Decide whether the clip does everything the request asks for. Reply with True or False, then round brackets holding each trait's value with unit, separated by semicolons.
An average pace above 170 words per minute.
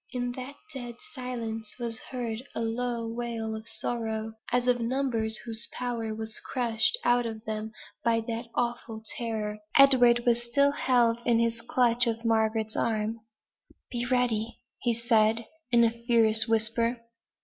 False (140 wpm)